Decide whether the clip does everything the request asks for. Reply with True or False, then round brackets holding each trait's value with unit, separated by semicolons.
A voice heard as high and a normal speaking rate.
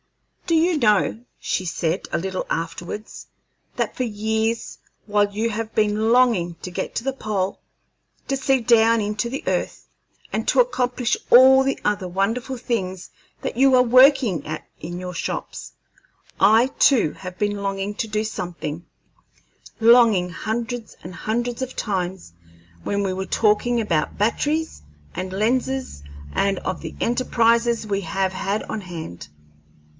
True (215 Hz; 150 wpm)